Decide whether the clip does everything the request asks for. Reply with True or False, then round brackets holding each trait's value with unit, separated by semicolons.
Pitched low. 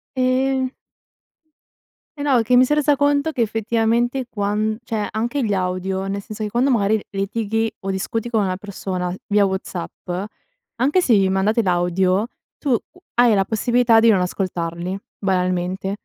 False (215 Hz)